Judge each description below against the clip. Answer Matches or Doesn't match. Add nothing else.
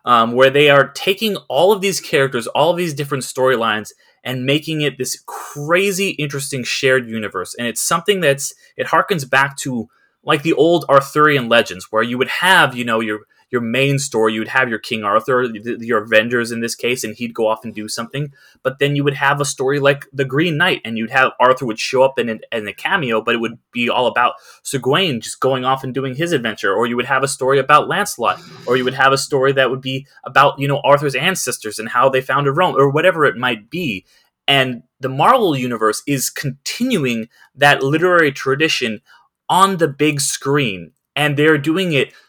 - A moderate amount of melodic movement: Matches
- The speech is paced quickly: Matches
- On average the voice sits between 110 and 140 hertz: Matches